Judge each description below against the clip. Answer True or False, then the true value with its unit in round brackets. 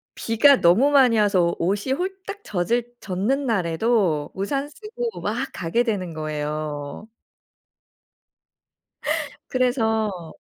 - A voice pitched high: True (220 Hz)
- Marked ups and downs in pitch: True (7.4 semitones)